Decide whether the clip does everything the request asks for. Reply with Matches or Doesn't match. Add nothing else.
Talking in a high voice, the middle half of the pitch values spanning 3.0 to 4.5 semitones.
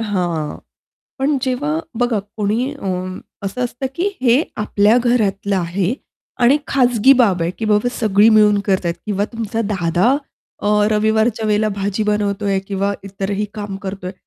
Matches